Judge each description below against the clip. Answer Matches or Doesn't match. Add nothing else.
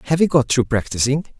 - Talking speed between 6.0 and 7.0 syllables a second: Matches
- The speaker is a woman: Doesn't match